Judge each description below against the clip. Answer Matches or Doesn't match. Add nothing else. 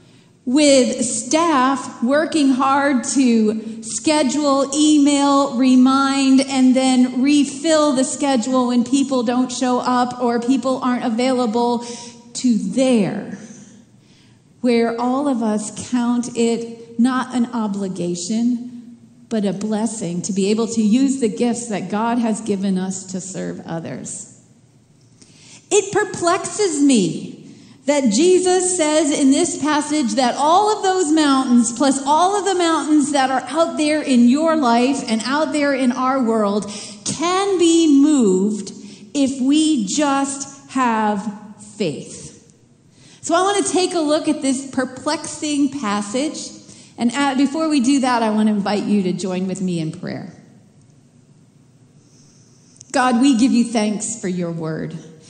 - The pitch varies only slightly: Doesn't match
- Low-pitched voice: Doesn't match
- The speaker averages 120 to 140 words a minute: Matches